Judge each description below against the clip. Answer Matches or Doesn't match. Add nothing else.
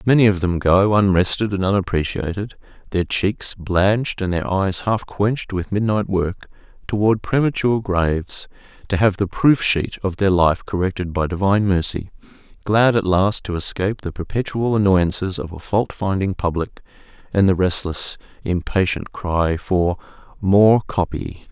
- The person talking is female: Doesn't match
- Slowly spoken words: Doesn't match